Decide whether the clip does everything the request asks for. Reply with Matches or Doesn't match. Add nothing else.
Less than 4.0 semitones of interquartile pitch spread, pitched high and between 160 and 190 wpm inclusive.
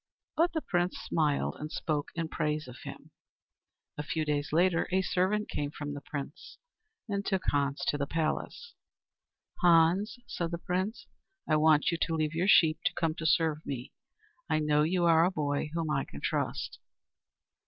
Doesn't match